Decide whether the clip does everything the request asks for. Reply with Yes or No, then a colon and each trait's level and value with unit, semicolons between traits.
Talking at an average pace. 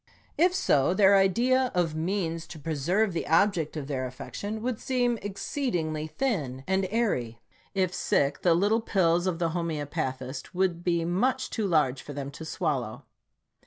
Yes: average, 160 wpm